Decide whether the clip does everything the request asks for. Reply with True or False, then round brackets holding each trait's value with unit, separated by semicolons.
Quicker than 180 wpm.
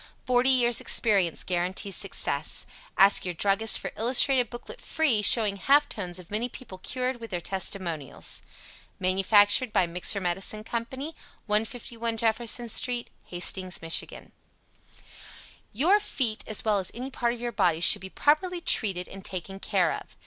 False (150 wpm)